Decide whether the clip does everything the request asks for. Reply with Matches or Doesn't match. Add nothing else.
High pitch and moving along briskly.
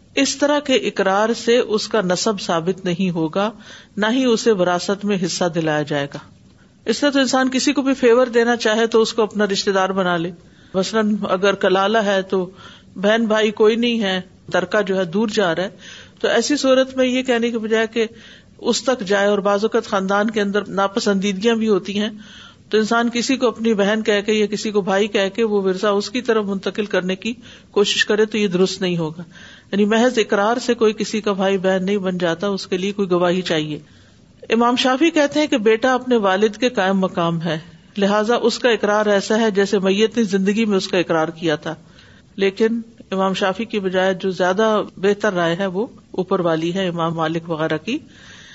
Matches